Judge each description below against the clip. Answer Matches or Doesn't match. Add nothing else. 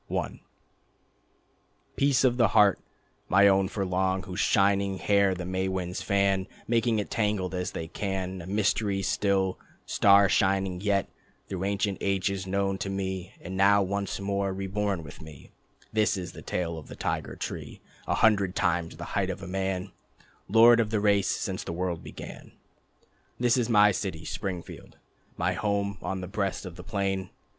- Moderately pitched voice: Doesn't match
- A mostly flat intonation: Matches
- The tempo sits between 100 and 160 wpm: Doesn't match